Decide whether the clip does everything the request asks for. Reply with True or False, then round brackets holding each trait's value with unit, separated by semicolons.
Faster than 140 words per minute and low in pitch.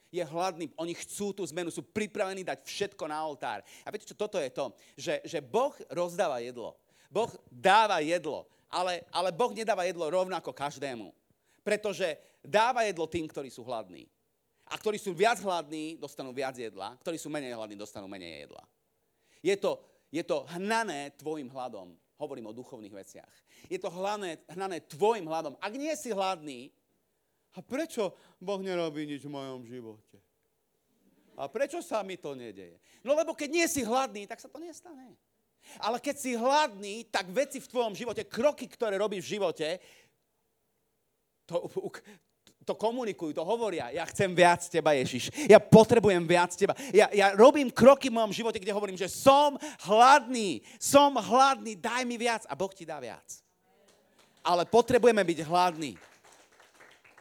False (160 wpm; 195 Hz)